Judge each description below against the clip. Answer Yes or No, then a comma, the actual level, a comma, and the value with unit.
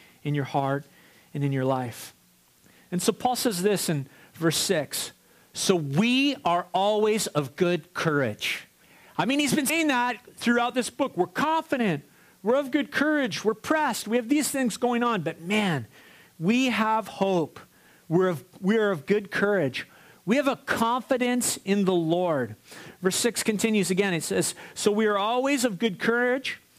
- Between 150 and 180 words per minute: Yes, average, 170 wpm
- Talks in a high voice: Yes, high, 205 Hz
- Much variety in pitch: Yes, wide, 6.4 semitones